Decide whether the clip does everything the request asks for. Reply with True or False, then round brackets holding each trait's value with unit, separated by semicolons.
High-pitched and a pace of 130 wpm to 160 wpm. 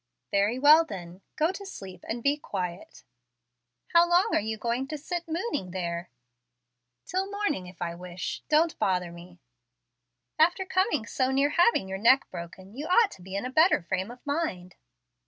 False (245 Hz; 175 wpm)